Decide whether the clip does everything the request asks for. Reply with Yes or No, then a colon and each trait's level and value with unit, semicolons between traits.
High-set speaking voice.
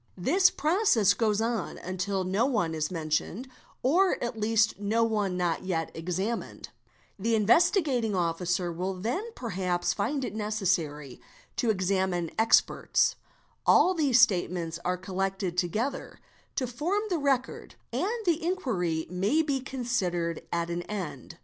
Yes: high, 205 Hz